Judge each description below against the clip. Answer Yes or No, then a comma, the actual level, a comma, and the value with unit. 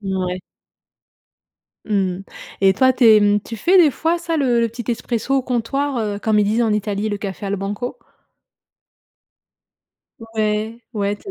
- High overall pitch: Yes, high, 220 Hz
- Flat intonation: No, average, 3.5 semitones